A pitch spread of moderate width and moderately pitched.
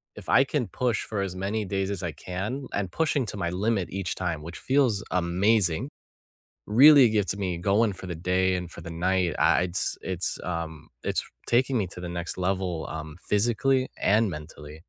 No: average, 4.1 semitones; very low, 95 Hz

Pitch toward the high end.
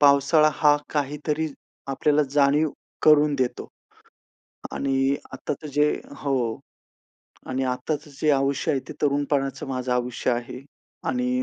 No: medium, 140 Hz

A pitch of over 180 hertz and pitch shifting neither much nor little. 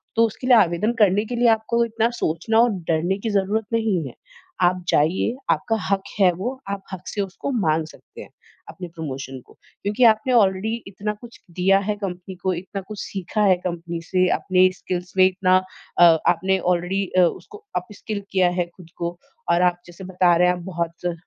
Yes: high, 190 Hz; average, 3.3 semitones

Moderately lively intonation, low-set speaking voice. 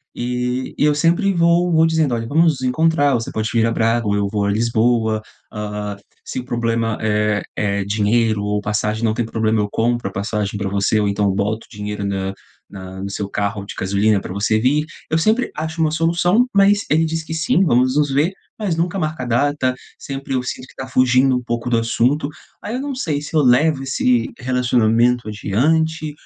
No: wide, 6.3 semitones; low, 120 Hz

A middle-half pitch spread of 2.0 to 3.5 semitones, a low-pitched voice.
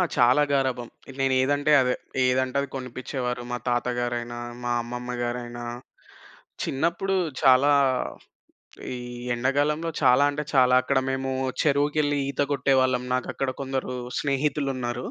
Yes: narrow, 2.4 semitones; low, 130 Hz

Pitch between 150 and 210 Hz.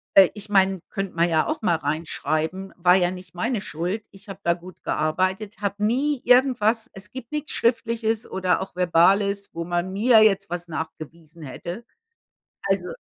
Yes: high, 190 Hz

